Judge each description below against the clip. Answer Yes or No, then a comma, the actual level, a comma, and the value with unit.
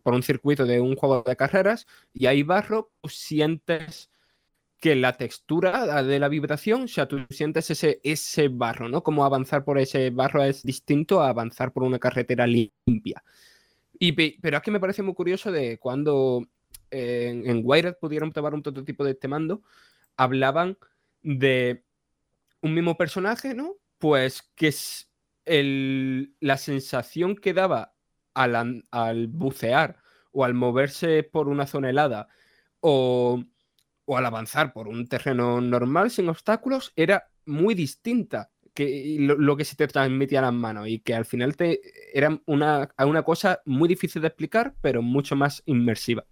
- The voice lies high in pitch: No, medium, 140 Hz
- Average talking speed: Yes, average, 160 wpm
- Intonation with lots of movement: No, average, 3.9 semitones